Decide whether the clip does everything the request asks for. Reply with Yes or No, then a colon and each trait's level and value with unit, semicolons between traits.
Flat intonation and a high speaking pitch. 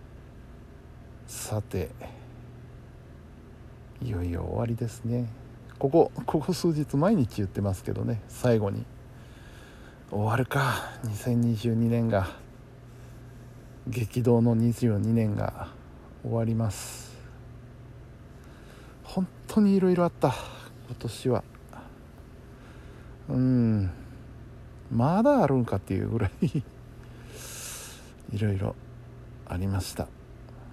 No: narrow, 1.8 semitones; low, 120 Hz